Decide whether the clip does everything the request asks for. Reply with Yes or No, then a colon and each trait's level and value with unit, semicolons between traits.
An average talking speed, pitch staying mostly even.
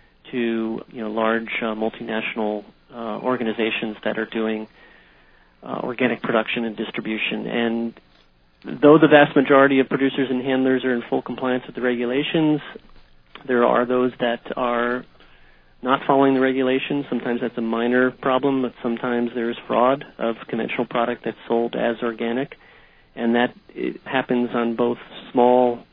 Yes: average, 150 wpm; narrow, 2.2 semitones